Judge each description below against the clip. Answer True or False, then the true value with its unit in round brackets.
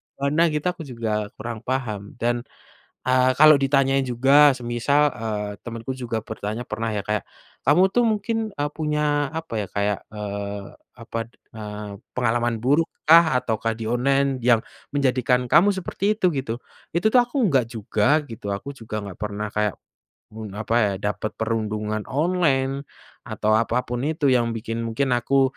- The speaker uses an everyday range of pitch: True (4.7 semitones)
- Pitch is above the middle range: False (120 Hz)